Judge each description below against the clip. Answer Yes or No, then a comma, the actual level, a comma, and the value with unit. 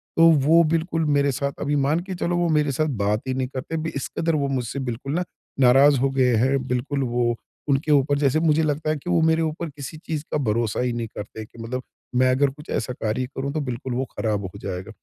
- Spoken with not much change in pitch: No, average, 3.7 semitones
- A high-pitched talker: No, medium, 140 Hz